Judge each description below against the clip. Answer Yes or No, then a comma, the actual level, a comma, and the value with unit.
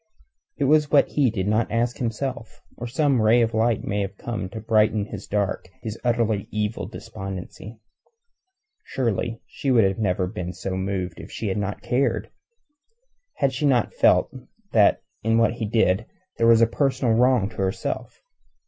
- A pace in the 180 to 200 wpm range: No, average, 165 wpm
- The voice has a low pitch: Yes, low, 110 Hz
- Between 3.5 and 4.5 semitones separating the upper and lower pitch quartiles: No, average, 2.9 semitones